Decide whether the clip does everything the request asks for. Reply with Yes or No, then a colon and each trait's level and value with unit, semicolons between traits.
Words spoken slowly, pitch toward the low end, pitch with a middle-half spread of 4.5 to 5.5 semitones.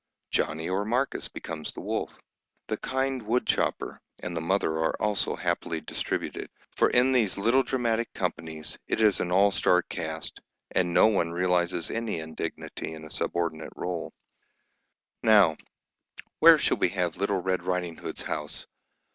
No: average, 150 wpm; very low, 90 Hz; average, 4.8 semitones